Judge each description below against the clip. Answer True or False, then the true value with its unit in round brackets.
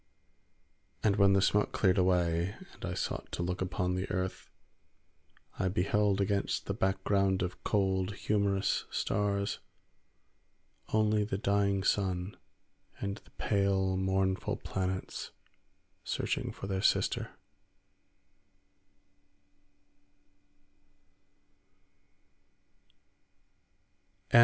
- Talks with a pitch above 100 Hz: False (95 Hz)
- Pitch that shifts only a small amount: True (1.3 semitones)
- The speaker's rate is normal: False (90 wpm)